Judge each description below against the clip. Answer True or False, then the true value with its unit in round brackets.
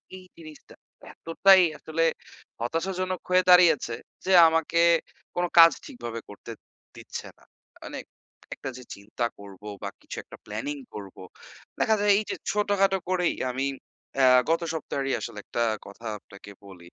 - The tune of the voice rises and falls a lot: True (7.9 semitones)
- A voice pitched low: False (150 Hz)